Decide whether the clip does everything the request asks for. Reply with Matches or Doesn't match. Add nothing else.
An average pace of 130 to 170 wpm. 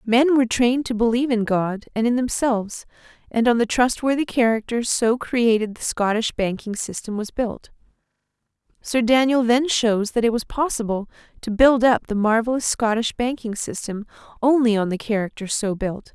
Matches